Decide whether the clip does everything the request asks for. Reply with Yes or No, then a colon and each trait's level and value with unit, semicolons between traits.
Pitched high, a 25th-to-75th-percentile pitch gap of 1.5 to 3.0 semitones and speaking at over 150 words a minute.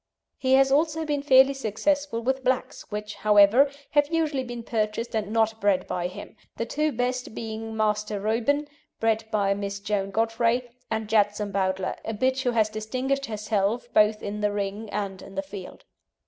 No: high, 220 Hz; average, 3.9 semitones; average, 175 wpm